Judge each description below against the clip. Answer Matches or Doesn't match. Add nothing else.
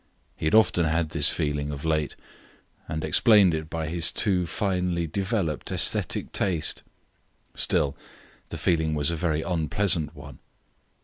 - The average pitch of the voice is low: Matches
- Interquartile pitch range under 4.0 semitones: Matches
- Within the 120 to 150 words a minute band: Matches